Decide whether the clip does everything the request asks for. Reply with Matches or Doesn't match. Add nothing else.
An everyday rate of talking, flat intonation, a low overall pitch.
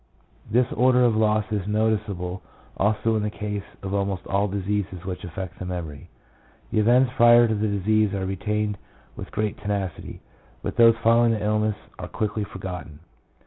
Matches